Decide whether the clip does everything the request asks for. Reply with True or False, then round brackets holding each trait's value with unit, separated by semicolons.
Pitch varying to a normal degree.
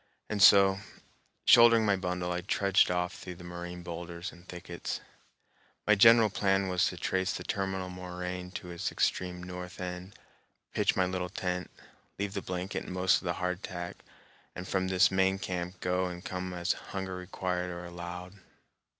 False (1.2 semitones)